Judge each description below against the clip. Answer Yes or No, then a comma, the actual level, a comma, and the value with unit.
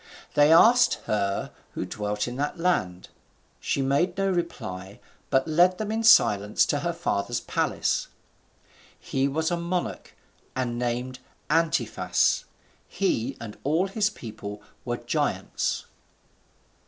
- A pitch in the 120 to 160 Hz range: Yes, low, 135 Hz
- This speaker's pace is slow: Yes, slow, 125 wpm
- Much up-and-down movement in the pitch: Yes, wide, 8.3 semitones